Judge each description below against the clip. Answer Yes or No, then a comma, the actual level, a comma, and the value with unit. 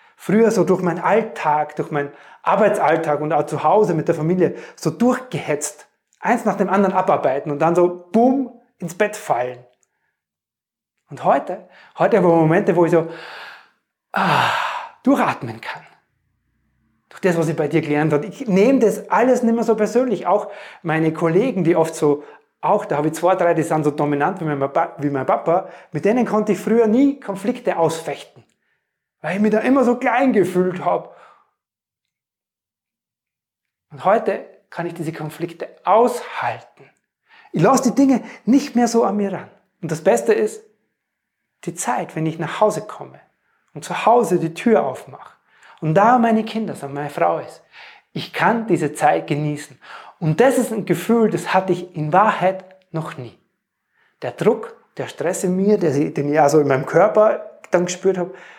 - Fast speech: No, average, 175 wpm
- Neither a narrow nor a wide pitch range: No, wide, 5.7 semitones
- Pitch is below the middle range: No, medium, 180 Hz